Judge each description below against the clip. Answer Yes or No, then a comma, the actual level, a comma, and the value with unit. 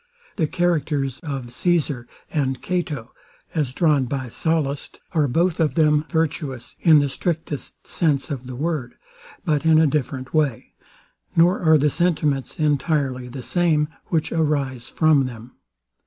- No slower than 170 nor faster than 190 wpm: No, average, 140 wpm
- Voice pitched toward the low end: No, medium, 150 Hz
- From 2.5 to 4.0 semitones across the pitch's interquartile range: Yes, average, 3.3 semitones